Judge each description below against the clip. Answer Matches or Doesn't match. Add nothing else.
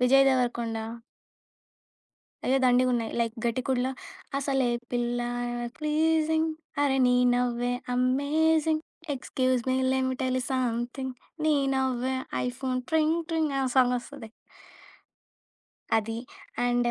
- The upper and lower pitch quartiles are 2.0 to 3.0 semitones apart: Matches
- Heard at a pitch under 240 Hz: Doesn't match